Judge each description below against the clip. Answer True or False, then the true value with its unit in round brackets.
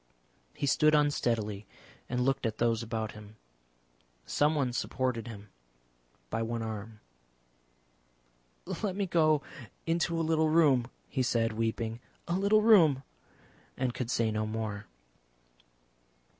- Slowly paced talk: True (120 wpm)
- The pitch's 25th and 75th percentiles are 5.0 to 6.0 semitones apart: True (5.6 semitones)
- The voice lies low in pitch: True (125 Hz)